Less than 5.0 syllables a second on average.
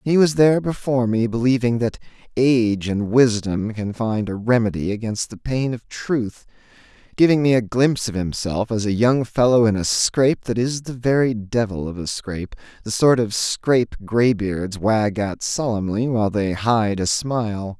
Yes: 4.8 syllables/s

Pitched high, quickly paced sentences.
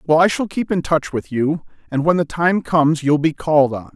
No: medium, 155 Hz; fast, 260 wpm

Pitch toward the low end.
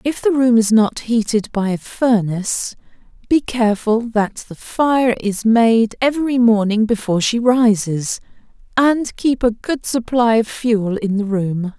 No: high, 225 Hz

